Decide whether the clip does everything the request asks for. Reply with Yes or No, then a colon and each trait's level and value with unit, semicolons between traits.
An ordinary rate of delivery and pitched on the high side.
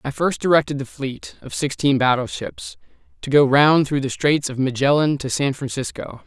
No: average, 180 wpm; medium, 140 Hz